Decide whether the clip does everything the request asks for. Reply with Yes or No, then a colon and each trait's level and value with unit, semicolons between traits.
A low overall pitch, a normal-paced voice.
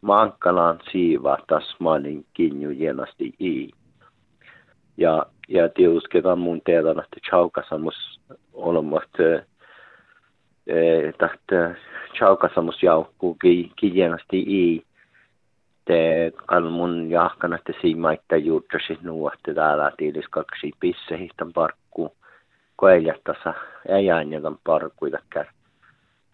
No: very low, 85 Hz; slow, 90 wpm